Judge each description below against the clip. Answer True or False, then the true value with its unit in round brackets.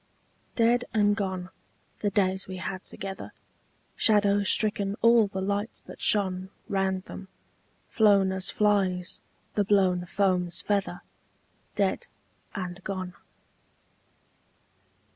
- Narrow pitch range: True (1.6 semitones)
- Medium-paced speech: False (105 wpm)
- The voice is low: False (195 Hz)